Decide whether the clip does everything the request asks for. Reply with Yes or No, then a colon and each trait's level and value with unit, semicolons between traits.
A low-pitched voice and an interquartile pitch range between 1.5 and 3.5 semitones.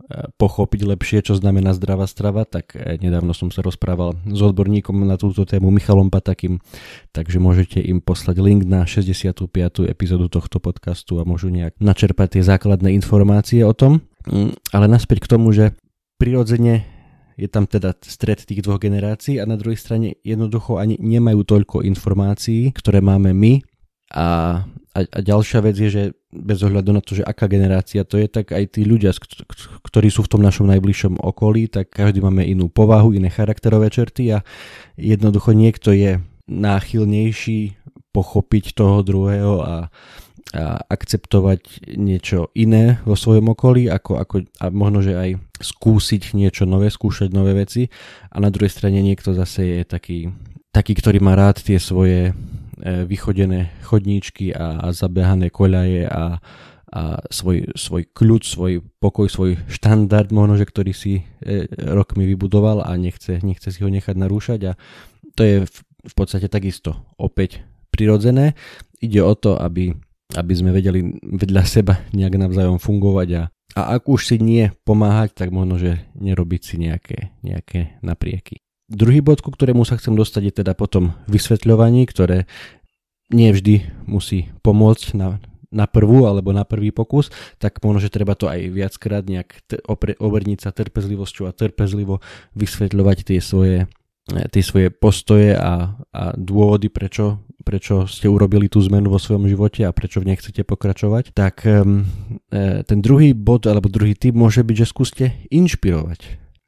Yes: low, 100 Hz; narrow, 2.4 semitones